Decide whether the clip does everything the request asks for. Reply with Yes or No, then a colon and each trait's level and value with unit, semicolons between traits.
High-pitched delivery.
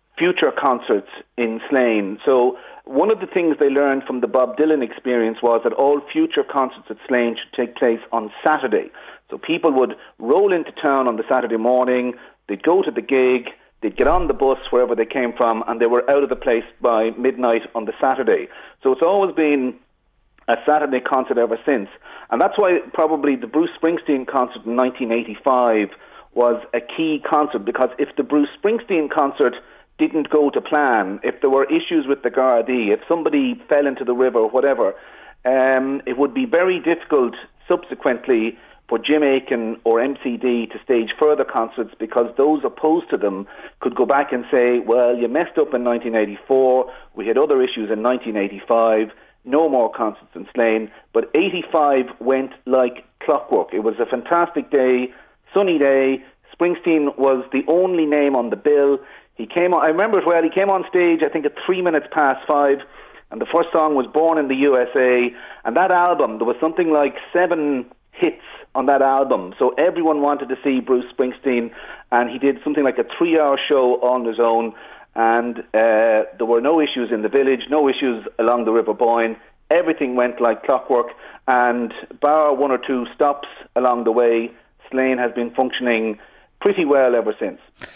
No: low, 135 Hz